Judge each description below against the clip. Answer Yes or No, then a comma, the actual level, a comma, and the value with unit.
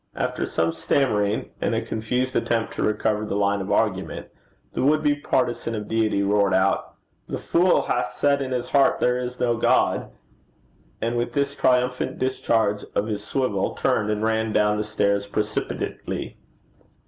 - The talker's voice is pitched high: No, low, 110 Hz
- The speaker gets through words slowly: No, average, 165 wpm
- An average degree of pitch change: Yes, average, 3.4 semitones